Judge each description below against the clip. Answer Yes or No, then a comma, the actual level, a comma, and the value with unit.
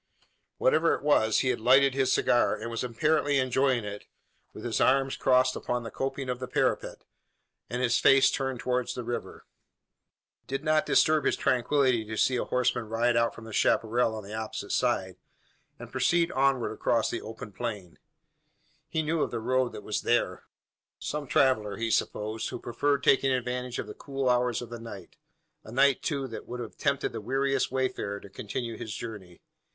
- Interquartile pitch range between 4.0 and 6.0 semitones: No, average, 3.1 semitones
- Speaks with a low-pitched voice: Yes, low, 125 Hz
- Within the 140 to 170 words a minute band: No, average, 190 wpm